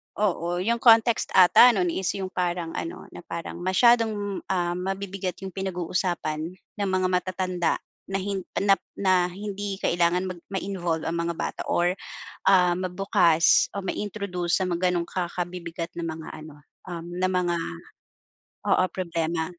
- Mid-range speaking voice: Yes, medium, 180 Hz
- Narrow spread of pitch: Yes, narrow, 1.9 semitones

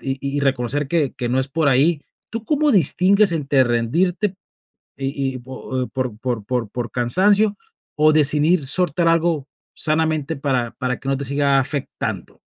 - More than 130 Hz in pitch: Yes, medium, 140 Hz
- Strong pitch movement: No, average, 4.2 semitones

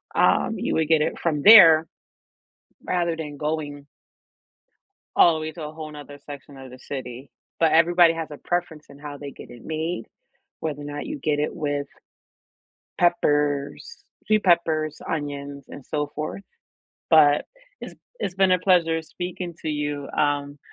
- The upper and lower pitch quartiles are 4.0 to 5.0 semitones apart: No, narrow, 2.4 semitones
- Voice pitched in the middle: Yes, medium, 155 Hz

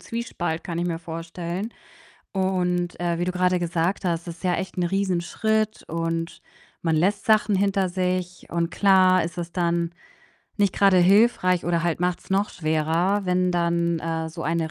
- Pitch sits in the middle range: Yes, medium, 175 Hz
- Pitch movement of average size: No, narrow, 2.0 semitones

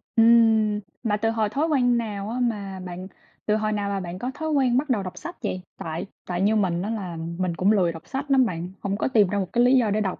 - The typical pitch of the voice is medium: No, high, 210 Hz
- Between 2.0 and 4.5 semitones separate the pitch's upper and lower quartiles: Yes, average, 4.1 semitones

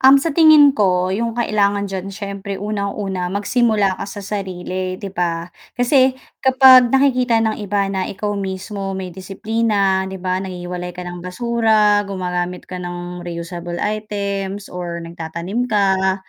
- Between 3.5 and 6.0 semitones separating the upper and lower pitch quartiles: No, average, 2.9 semitones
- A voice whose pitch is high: Yes, high, 195 Hz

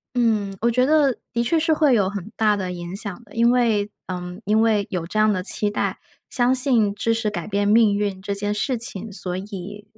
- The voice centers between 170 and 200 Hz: No, high, 210 Hz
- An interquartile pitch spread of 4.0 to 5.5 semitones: No, average, 2.9 semitones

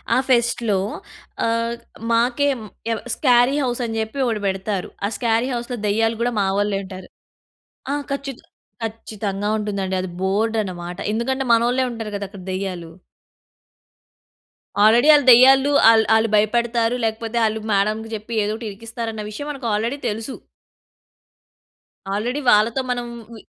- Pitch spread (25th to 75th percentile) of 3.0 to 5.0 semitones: No, narrow, 2.5 semitones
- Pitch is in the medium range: No, high, 225 Hz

